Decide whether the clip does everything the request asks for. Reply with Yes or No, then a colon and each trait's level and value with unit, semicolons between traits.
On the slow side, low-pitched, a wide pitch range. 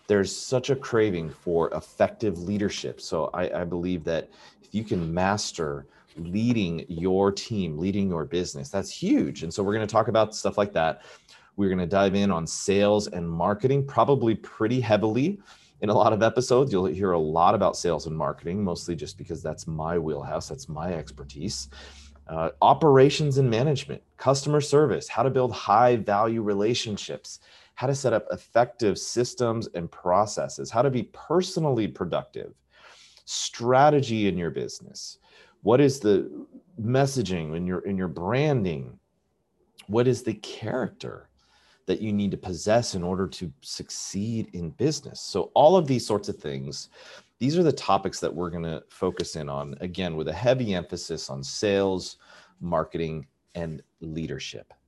No: average, 165 wpm; low, 100 Hz; wide, 6.1 semitones